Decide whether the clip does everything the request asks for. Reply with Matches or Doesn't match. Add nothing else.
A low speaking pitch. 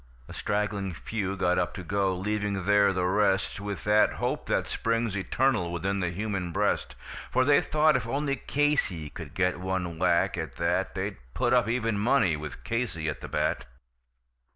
Matches